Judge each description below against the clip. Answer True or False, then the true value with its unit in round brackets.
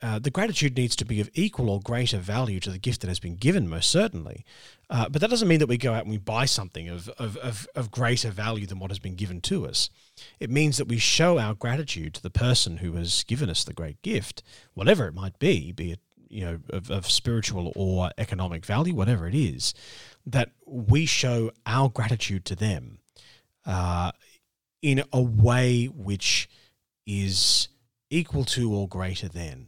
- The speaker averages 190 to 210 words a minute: True (200 wpm)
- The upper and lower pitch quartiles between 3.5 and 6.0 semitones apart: True (4.9 semitones)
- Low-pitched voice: True (115 Hz)